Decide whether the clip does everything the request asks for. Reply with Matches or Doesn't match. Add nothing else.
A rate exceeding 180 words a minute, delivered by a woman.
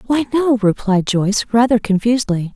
Doesn't match